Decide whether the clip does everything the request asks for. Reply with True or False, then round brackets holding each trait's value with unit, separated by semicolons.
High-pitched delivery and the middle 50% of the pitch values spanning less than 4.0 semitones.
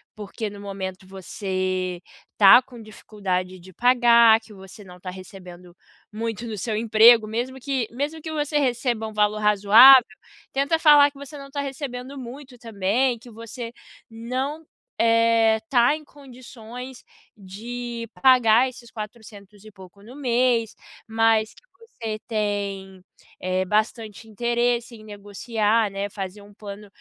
True (225 Hz; 3.4 semitones)